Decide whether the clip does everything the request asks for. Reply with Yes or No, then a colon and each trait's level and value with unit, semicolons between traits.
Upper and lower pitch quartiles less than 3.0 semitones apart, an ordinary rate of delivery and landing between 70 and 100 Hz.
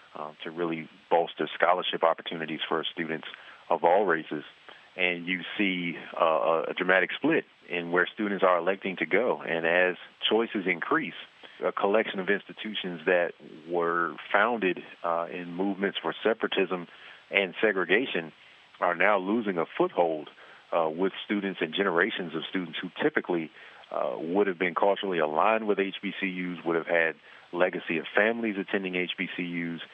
Yes: narrow, 2.4 semitones; average, 145 wpm; very low, 90 Hz